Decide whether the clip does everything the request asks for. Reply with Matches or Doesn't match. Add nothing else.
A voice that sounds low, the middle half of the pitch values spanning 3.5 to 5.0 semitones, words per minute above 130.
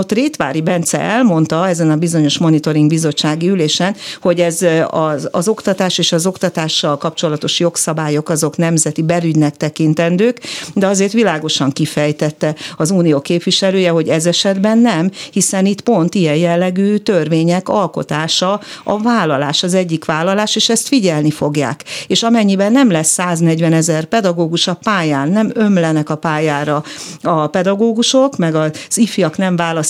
Doesn't match